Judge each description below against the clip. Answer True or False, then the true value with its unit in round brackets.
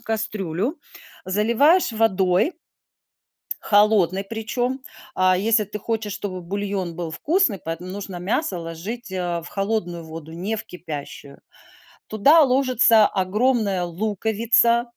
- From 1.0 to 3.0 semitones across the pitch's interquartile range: False (4.0 semitones)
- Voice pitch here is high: True (205 Hz)